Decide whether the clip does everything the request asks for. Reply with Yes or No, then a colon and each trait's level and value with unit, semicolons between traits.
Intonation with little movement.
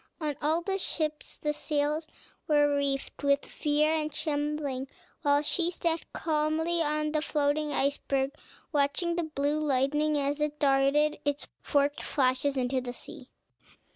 Yes: narrow, 1.5 semitones